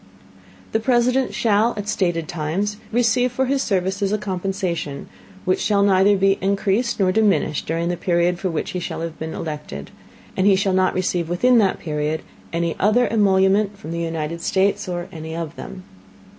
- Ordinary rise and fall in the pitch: Yes, average, 3.5 semitones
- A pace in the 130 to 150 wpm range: No, average, 175 wpm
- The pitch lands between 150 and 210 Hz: Yes, high, 190 Hz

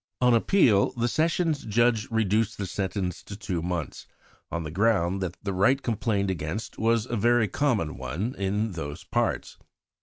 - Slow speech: No, average, 160 wpm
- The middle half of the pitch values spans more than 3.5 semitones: Yes, average, 4.0 semitones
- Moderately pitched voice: No, low, 105 Hz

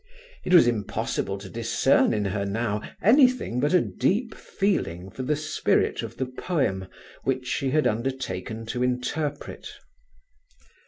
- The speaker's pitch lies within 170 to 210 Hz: No, low, 125 Hz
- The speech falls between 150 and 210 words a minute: No, average, 140 wpm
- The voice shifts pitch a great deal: Yes, wide, 6.2 semitones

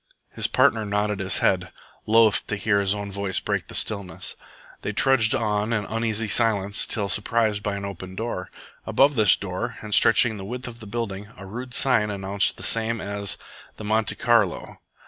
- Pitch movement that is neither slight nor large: No, narrow, 2.2 semitones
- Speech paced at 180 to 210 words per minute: Yes, average, 185 wpm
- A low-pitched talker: Yes, low, 105 Hz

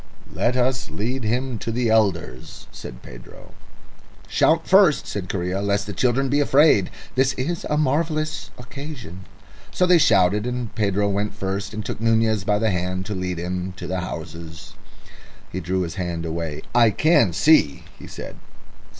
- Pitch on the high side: No, low, 105 Hz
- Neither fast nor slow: Yes, average, 165 wpm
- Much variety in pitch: Yes, wide, 6.0 semitones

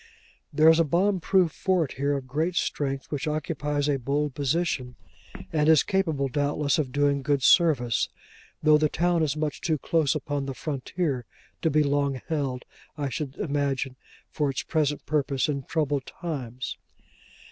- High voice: No, medium, 145 Hz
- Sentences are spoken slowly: No, average, 160 wpm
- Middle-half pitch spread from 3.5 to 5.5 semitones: No, narrow, 2.5 semitones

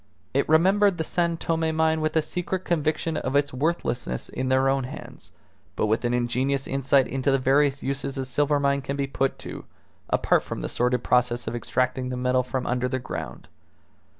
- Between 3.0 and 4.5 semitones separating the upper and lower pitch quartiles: Yes, average, 3.5 semitones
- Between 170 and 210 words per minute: Yes, average, 195 wpm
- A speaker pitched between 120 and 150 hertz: Yes, low, 135 Hz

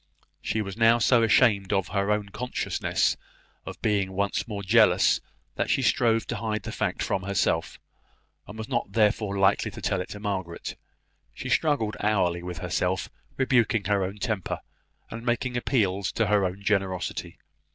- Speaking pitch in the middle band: No, low, 105 Hz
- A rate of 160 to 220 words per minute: Yes, average, 165 wpm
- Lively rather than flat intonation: No, average, 2.8 semitones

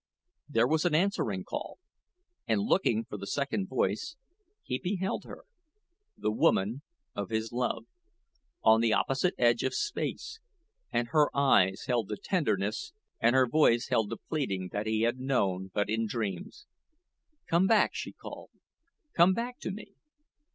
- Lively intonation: Yes, wide, 6.9 semitones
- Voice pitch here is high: No, low, 120 Hz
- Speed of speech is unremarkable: Yes, average, 150 wpm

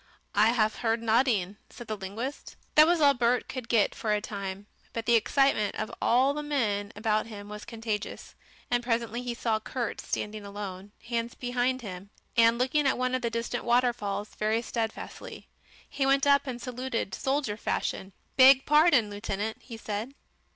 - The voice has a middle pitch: No, high, 230 Hz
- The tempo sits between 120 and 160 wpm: No, average, 170 wpm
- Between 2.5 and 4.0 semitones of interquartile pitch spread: Yes, average, 3.3 semitones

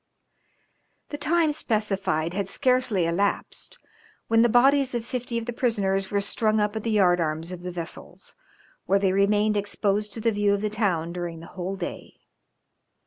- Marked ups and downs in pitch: No, average, 3.7 semitones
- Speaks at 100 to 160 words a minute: No, average, 175 wpm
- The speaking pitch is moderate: No, high, 205 Hz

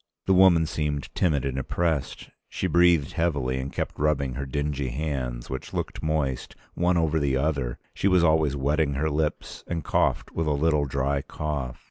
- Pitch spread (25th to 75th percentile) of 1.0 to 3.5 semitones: Yes, average, 2.8 semitones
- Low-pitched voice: Yes, very low, 75 Hz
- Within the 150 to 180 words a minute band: Yes, average, 175 wpm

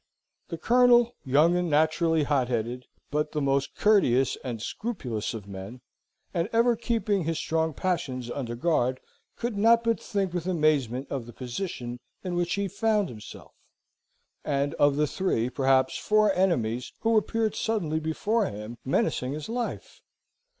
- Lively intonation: Yes, wide, 7.9 semitones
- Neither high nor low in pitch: Yes, medium, 155 Hz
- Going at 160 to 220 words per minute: No, average, 150 wpm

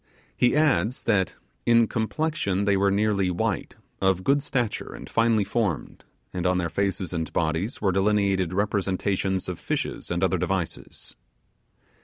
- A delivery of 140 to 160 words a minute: Yes, average, 145 wpm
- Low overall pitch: Yes, low, 100 Hz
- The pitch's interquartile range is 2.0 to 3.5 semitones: Yes, average, 3.0 semitones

